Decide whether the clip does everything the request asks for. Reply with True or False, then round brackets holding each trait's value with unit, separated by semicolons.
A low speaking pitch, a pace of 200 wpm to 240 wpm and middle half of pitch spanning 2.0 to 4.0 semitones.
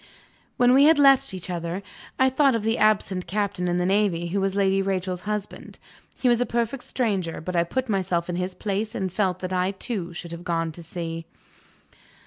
False (190 Hz; 205 wpm; 3.7 semitones)